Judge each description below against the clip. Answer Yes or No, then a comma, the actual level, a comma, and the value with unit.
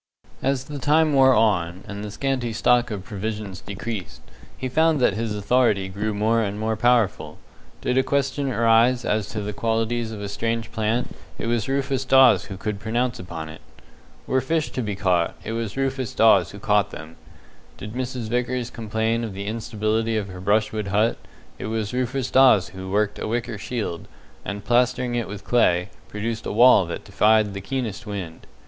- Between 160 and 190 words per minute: Yes, average, 185 wpm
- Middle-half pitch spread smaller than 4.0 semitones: Yes, average, 3.3 semitones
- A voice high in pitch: No, low, 110 Hz